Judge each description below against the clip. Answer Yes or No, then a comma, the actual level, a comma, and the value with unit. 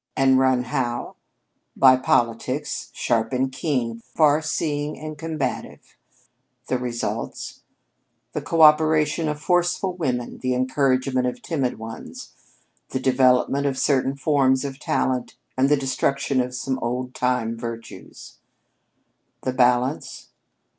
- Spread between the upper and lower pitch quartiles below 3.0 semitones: Yes, narrow, 2.6 semitones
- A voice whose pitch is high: No, low, 130 Hz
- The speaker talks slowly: Yes, slow, 120 wpm